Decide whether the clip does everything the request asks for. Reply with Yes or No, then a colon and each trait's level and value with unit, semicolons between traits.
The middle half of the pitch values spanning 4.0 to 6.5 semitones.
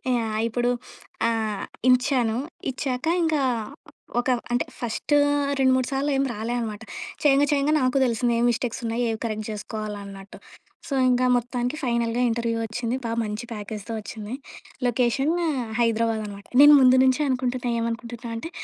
No: narrow, 2.4 semitones